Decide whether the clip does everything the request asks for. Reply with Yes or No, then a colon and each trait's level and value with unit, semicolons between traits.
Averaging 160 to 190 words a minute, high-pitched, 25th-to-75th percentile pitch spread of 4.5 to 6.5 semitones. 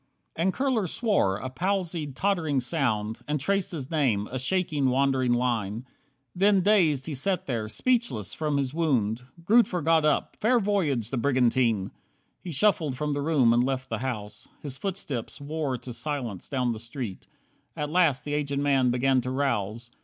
No: average, 170 wpm; medium, 140 Hz; average, 5.2 semitones